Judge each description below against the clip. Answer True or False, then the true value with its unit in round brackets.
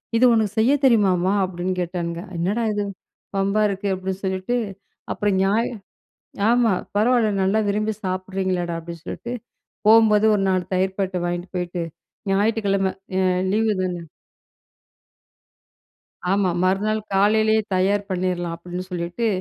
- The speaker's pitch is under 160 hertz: False (195 Hz)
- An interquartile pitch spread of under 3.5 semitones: True (2.8 semitones)